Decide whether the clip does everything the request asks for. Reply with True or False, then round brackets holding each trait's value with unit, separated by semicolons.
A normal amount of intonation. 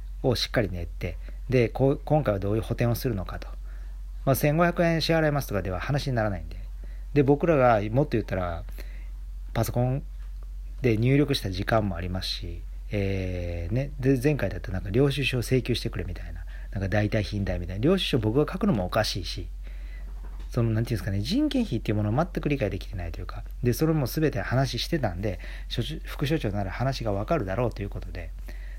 False (7.1 semitones)